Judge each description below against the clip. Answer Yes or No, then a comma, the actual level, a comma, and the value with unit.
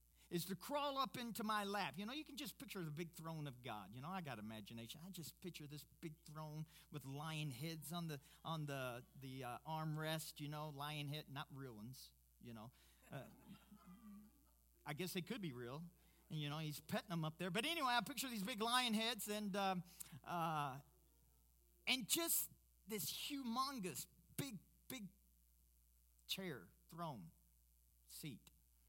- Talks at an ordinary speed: Yes, average, 170 wpm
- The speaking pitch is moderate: Yes, medium, 155 Hz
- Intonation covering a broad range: Yes, wide, 7.7 semitones